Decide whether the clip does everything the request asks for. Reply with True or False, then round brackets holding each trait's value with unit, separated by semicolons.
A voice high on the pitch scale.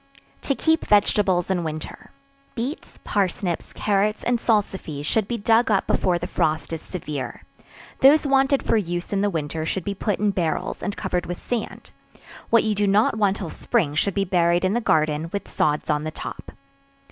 True (195 Hz)